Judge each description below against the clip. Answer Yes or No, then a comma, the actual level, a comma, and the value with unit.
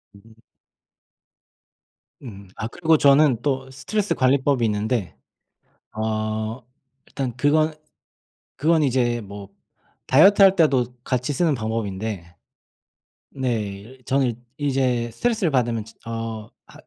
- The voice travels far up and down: No, average, 4.4 semitones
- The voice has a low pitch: Yes, low, 125 Hz